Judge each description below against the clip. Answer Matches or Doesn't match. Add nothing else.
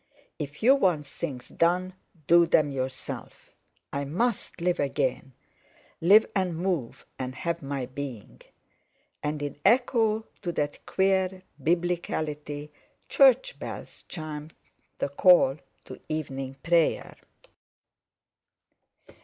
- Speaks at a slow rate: Matches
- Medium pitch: Matches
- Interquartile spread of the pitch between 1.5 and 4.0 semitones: Doesn't match